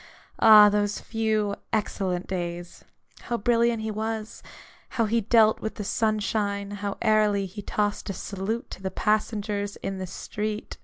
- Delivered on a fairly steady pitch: Yes, narrow, 1.5 semitones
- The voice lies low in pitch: No, high, 210 Hz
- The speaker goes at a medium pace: Yes, average, 150 wpm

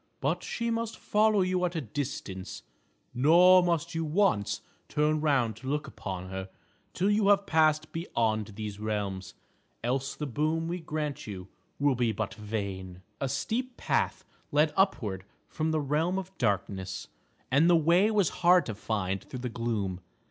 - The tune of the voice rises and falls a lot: Yes, wide, 8.3 semitones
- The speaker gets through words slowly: No, average, 165 wpm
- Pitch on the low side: No, medium, 145 Hz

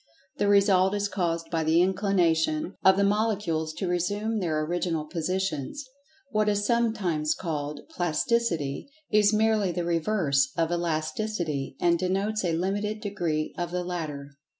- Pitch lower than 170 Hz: No, medium, 180 Hz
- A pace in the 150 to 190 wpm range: No, average, 140 wpm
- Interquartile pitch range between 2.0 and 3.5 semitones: No, average, 4.2 semitones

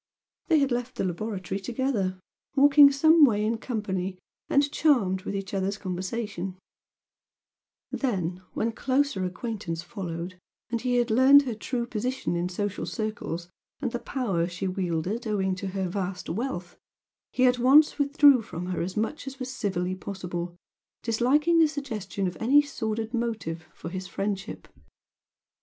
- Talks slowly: No, average, 150 wpm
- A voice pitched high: Yes, high, 215 Hz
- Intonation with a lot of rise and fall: Yes, wide, 5.7 semitones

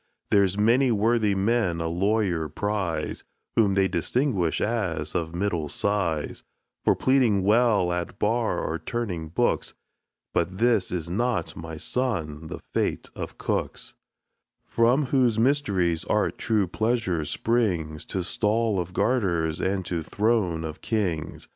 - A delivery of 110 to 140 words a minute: Yes, slow, 135 wpm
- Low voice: Yes, low, 100 Hz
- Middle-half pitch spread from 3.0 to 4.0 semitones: No, average, 5.3 semitones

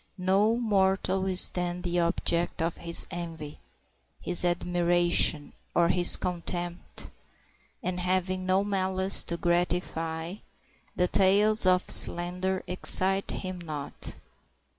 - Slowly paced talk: Yes, slow, 110 wpm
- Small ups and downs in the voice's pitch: Yes, narrow, 1.5 semitones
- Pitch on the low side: No, medium, 180 Hz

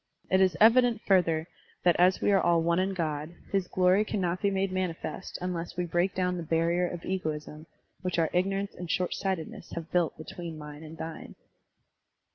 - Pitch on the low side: No, medium, 180 Hz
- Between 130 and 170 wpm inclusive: No, average, 180 wpm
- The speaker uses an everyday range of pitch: No, narrow, 2.3 semitones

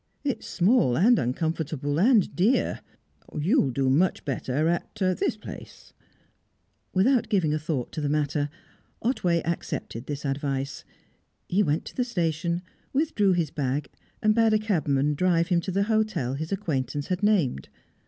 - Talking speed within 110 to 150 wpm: Yes, average, 145 wpm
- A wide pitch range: Yes, wide, 6.0 semitones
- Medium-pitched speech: Yes, medium, 165 Hz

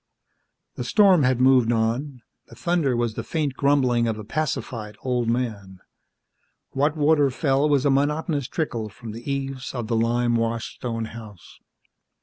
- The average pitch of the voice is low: Yes, low, 125 Hz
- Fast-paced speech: No, average, 155 wpm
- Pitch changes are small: No, average, 3.7 semitones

